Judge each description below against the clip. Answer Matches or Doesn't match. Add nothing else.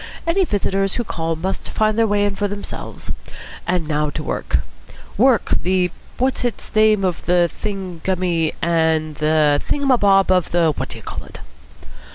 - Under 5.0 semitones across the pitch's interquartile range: Matches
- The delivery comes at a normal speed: Matches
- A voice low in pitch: Doesn't match